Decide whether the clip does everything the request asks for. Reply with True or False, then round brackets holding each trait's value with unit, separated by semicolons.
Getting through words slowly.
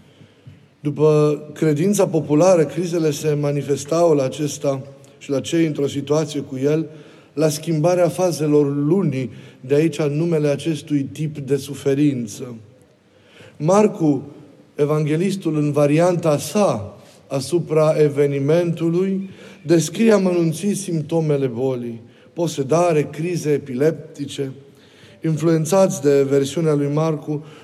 True (100 wpm)